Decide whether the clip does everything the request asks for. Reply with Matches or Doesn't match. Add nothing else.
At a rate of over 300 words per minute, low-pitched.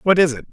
Doesn't match